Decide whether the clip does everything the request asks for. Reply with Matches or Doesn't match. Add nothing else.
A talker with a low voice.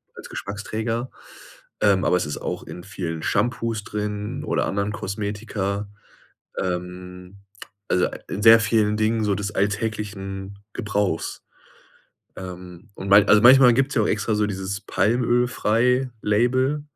Matches